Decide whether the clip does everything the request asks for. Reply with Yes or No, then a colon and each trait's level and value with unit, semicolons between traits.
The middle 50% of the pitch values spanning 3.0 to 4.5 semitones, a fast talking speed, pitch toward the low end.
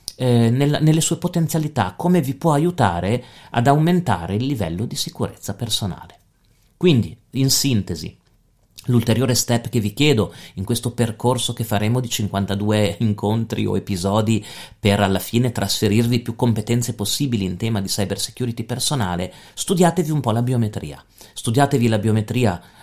No: average, 4.1 semitones; average, 145 wpm; low, 115 Hz